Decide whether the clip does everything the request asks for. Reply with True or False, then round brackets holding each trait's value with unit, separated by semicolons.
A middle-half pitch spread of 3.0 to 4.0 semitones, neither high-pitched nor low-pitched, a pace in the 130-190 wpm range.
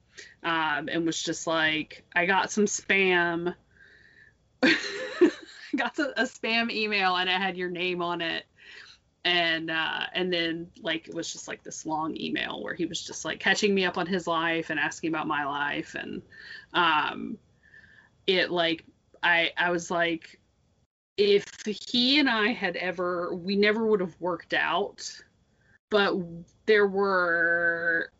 True (3.7 semitones; 180 Hz; 155 wpm)